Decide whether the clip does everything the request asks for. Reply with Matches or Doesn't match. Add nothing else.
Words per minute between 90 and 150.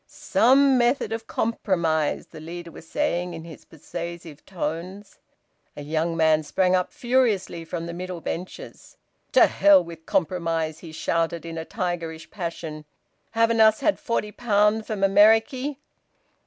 Matches